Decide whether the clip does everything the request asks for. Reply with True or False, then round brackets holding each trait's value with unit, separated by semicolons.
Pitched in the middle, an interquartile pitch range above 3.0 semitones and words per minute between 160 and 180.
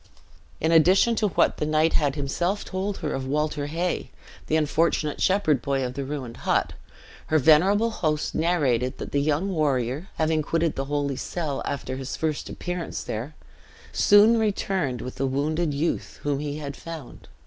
True (155 Hz; 3.5 semitones; 170 wpm)